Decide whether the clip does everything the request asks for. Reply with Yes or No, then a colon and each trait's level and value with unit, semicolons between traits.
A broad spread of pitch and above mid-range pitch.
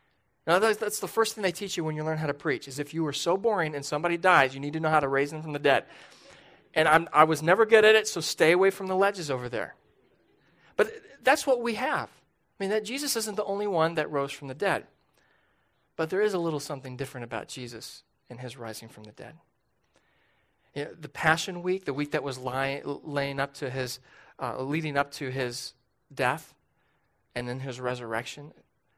No: wide, 5.9 semitones; medium, 150 Hz